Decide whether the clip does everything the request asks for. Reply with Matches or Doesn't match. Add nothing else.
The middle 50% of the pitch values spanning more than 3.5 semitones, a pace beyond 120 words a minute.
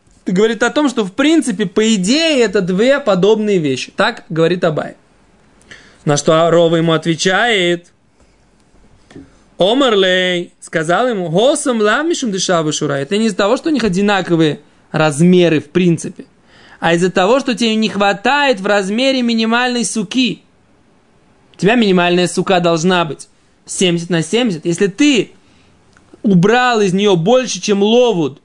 Matches